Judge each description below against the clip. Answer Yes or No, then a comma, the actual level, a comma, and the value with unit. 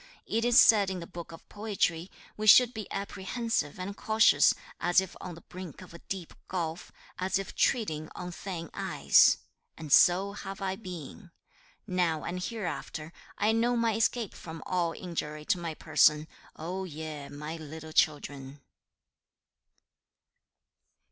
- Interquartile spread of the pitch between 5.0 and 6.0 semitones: No, average, 4.0 semitones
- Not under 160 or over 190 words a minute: No, average, 150 wpm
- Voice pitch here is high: No, medium, 180 Hz